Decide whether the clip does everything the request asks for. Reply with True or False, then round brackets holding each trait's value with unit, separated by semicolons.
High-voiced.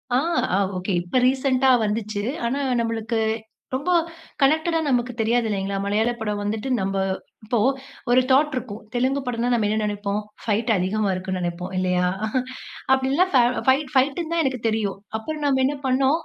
True (235 Hz)